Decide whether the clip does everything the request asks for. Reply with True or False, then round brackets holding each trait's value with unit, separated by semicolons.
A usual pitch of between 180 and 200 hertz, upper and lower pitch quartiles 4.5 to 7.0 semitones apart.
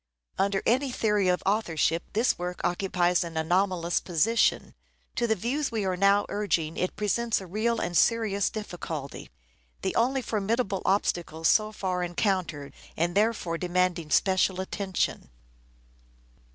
False (190 Hz; 3.6 semitones)